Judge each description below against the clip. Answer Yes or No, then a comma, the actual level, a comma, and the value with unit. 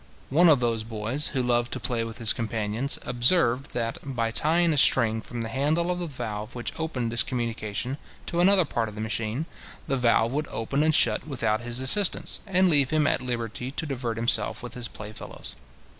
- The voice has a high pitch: No, low, 120 Hz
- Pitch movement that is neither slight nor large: Yes, average, 4.3 semitones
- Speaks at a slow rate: No, fast, 205 wpm